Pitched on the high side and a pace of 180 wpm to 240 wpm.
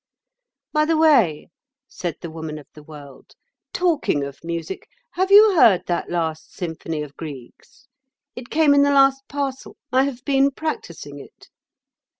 No: high, 200 Hz; average, 150 wpm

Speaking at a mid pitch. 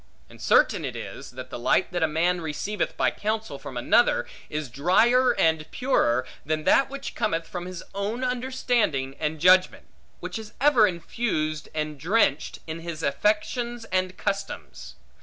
Yes: medium, 180 Hz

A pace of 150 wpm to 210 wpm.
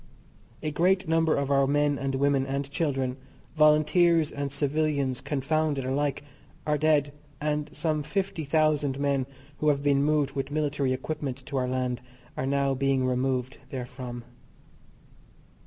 No: average, 140 wpm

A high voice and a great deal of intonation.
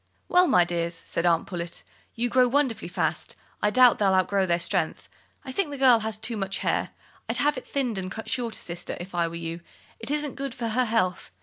Yes: high, 220 Hz; wide, 6.3 semitones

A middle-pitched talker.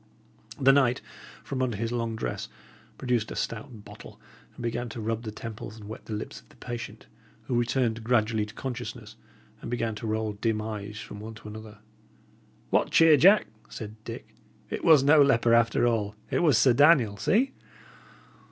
No: low, 115 Hz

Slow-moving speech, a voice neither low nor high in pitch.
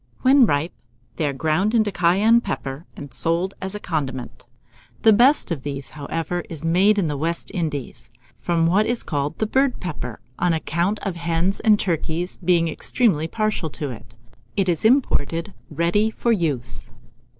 No: average, 165 wpm; medium, 170 Hz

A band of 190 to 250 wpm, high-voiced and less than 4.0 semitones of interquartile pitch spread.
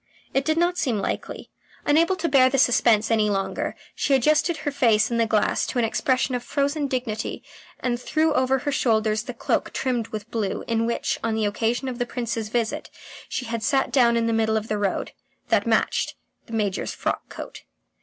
Yes: average, 200 wpm; high, 240 Hz; average, 3.5 semitones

